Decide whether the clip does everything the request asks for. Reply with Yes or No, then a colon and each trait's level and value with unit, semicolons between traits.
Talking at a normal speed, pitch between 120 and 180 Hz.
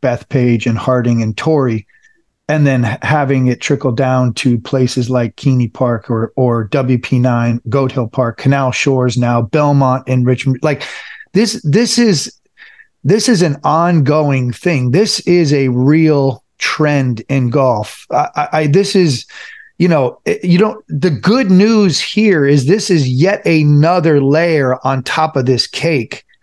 Yes: average, 155 wpm; medium, 140 Hz